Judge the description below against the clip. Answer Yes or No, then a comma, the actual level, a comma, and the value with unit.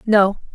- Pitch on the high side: Yes, high, 205 Hz